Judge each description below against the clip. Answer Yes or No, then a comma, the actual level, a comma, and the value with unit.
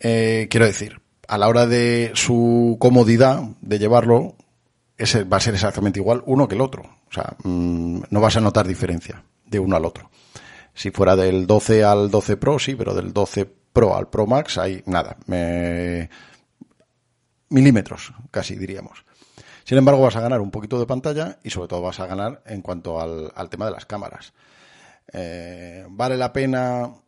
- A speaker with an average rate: Yes, average, 180 wpm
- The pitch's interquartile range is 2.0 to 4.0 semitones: No, average, 4.4 semitones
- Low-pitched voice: Yes, low, 110 Hz